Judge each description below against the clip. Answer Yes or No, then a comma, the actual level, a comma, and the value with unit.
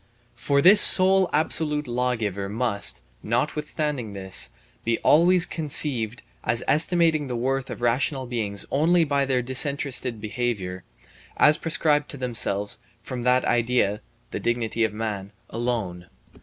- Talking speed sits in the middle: No, slow, 130 wpm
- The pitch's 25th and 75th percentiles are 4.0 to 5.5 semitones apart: Yes, average, 4.9 semitones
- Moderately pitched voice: No, low, 125 Hz